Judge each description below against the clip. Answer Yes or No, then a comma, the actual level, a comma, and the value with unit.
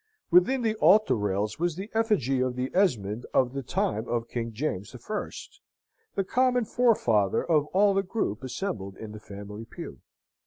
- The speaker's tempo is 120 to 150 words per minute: No, average, 170 wpm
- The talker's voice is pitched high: No, low, 130 Hz